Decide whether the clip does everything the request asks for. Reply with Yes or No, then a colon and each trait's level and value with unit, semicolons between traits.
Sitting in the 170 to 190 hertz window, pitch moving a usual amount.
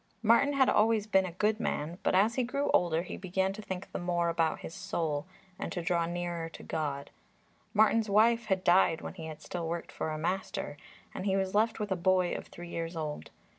Yes: medium, 185 Hz; average, 3.8 semitones